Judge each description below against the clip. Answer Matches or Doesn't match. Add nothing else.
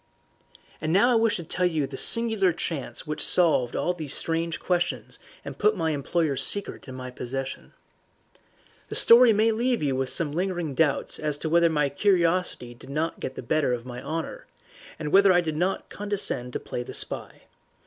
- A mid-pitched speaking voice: Matches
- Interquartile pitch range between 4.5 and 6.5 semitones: Matches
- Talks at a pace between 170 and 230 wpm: Matches